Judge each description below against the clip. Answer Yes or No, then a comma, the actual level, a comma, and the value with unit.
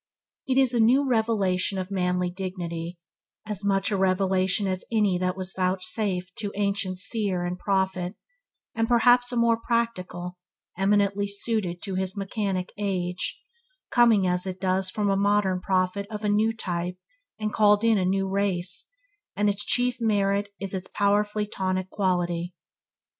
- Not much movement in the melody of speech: Yes, narrow, 2.3 semitones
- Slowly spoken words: No, average, 155 wpm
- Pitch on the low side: No, high, 195 Hz